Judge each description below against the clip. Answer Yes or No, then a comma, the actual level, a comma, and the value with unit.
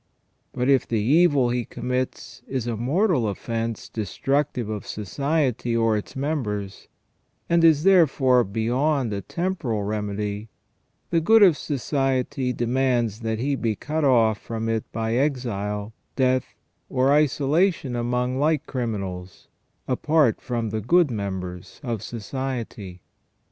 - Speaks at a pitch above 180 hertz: No, low, 125 Hz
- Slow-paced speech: Yes, slow, 130 wpm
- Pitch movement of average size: Yes, average, 4.2 semitones